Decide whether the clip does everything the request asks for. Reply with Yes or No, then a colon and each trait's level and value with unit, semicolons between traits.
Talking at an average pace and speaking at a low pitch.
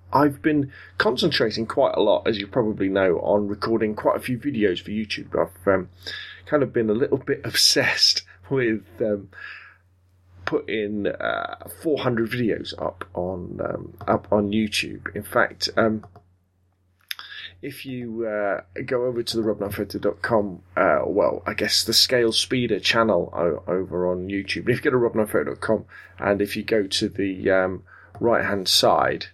Yes: average, 155 wpm; low, 105 Hz